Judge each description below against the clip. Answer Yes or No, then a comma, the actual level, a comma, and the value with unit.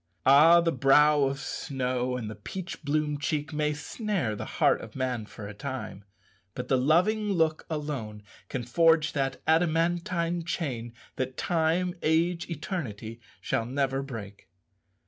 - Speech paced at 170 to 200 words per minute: No, average, 145 wpm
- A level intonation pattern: No, average, 4.8 semitones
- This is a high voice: No, medium, 150 Hz